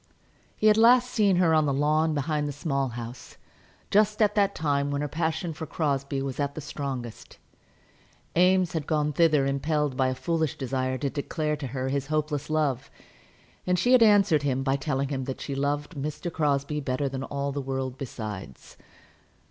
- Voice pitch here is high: No, medium, 145 Hz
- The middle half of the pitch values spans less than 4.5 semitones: Yes, average, 2.9 semitones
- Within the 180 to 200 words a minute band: Yes, average, 185 wpm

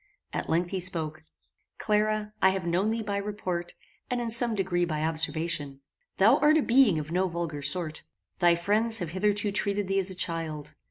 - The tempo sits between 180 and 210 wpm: Yes, average, 185 wpm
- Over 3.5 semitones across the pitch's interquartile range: Yes, average, 4.0 semitones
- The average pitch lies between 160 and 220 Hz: Yes, medium, 185 Hz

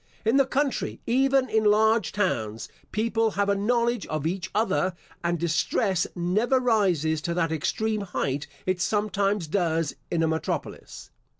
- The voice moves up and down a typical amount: Yes, average, 4.6 semitones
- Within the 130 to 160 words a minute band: Yes, average, 145 wpm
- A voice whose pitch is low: No, high, 200 Hz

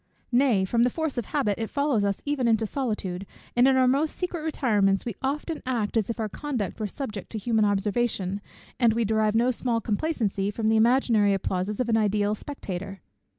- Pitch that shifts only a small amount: No, average, 4.0 semitones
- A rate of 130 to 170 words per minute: No, average, 195 wpm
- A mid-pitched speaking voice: No, high, 225 Hz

